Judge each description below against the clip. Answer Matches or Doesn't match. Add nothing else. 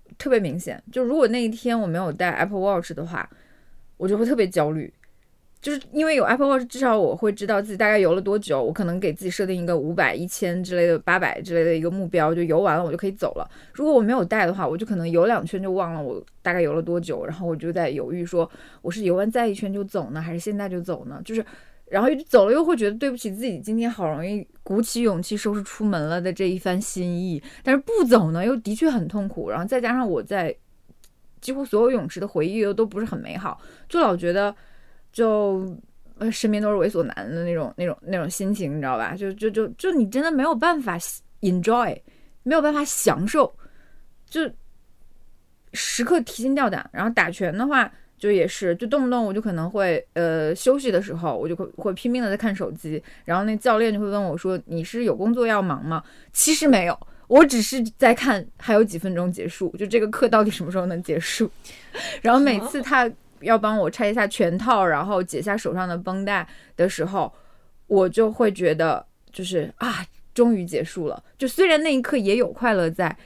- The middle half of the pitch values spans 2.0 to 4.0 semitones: Doesn't match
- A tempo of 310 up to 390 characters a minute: Matches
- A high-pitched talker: Matches